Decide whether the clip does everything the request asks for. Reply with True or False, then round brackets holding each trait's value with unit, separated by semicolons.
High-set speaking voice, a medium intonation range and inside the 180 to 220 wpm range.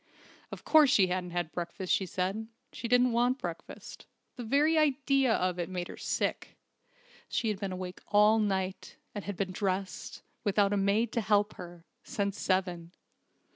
False (200 Hz; 3.6 semitones; 170 wpm)